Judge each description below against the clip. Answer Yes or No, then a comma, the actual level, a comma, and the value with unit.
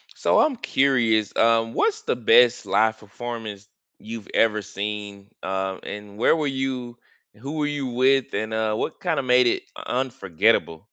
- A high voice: No, low, 115 Hz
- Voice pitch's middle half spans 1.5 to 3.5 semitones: No, average, 3.9 semitones